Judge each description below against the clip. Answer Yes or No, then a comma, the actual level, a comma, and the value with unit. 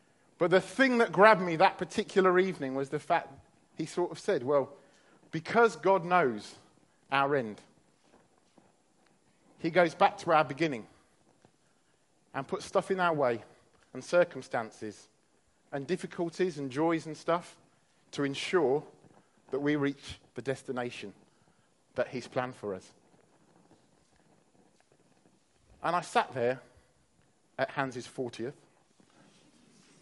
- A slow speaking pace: Yes, slow, 120 wpm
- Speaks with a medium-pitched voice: Yes, medium, 155 Hz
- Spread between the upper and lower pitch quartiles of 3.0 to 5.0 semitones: No, wide, 5.6 semitones